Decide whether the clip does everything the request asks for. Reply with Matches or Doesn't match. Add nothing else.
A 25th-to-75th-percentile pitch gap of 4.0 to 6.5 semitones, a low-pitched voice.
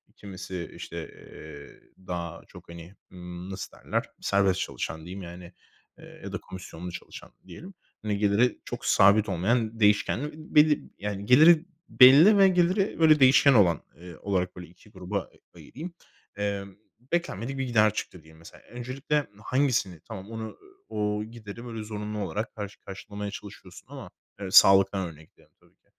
Matches